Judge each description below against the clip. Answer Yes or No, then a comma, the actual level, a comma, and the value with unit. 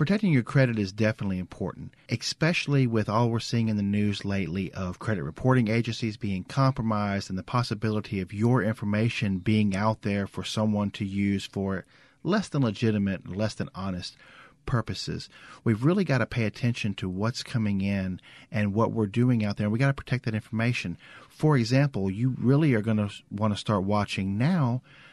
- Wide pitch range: No, average, 3.7 semitones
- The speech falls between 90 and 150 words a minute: No, average, 180 wpm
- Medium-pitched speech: No, low, 110 Hz